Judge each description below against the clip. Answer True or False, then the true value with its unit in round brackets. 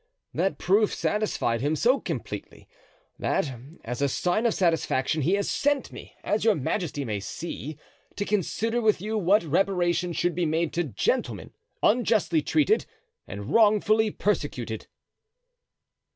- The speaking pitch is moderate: True (180 Hz)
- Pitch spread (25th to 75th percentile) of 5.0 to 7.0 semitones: True (5.4 semitones)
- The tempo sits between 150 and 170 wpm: False (135 wpm)